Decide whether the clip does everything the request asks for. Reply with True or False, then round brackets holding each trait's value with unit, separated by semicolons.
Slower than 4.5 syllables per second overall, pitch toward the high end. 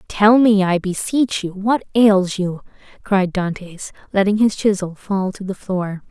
True (4.0 syllables/s; 195 Hz)